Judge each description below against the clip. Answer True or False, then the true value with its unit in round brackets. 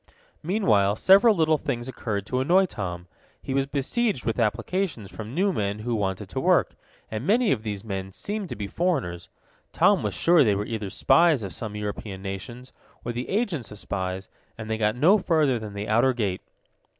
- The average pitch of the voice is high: False (115 Hz)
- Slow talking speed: False (190 wpm)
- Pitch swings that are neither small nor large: False (7.8 semitones)